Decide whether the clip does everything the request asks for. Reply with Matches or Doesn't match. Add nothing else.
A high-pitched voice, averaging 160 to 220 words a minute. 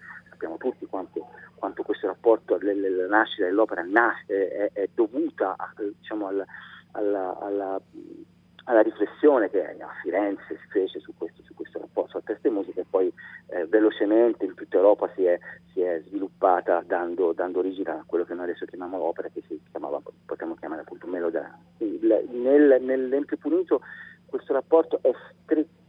Matches